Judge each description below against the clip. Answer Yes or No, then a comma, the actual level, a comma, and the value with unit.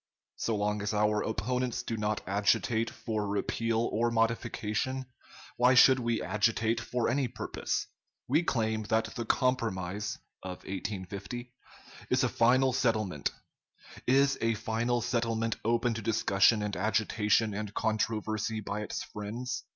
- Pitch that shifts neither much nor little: No, narrow, 2.1 semitones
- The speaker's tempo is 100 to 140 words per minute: Yes, slow, 135 wpm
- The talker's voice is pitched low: Yes, low, 110 Hz